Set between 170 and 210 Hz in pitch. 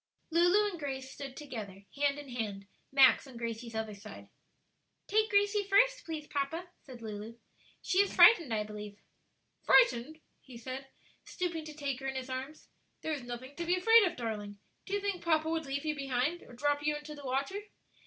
No: very high, 280 Hz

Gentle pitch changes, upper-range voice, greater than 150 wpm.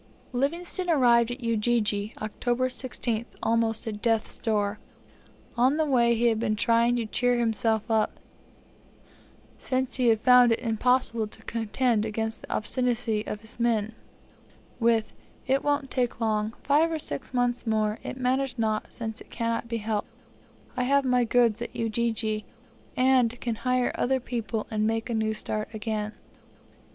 Yes: narrow, 2.2 semitones; high, 235 Hz; average, 160 wpm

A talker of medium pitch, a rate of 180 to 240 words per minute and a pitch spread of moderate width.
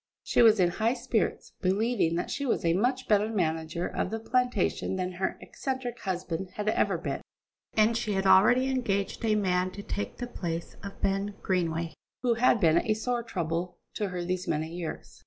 No: high, 200 Hz; average, 190 wpm; average, 4.4 semitones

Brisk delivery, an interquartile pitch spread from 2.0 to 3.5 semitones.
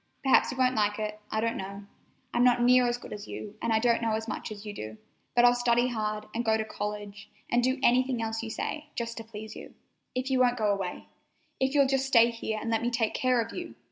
Yes: fast, 255 wpm; narrow, 2.5 semitones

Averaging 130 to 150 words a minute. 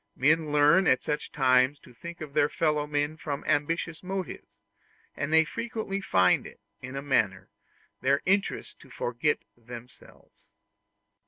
Yes: average, 145 wpm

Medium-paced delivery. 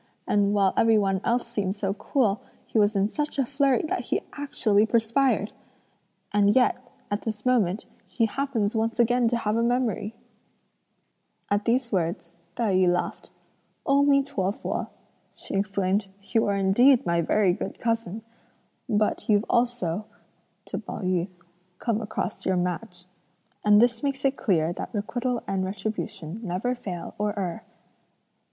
Yes: average, 155 wpm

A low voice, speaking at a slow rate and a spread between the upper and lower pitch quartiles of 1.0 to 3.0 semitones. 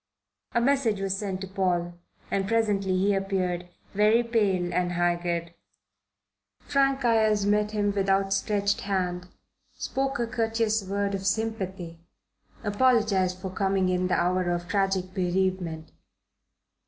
No: high, 195 Hz; slow, 130 wpm; narrow, 2.6 semitones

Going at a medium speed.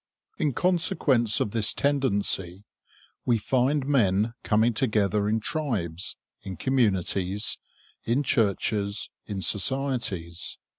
No: slow, 100 wpm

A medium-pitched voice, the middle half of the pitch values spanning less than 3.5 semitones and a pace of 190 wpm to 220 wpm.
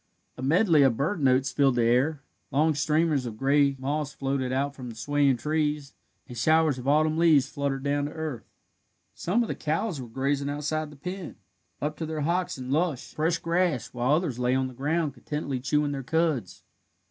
Yes: medium, 145 Hz; average, 2.9 semitones; average, 195 wpm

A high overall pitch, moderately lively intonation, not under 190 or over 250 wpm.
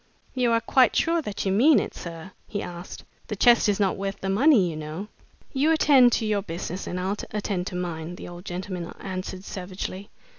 Yes: high, 195 Hz; average, 4.2 semitones; average, 200 wpm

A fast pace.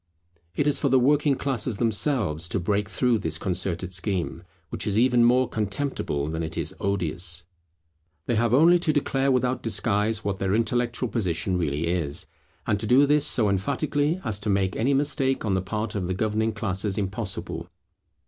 No: average, 175 wpm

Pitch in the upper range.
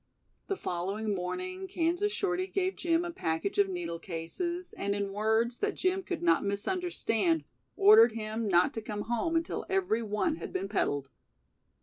Yes: high, 230 Hz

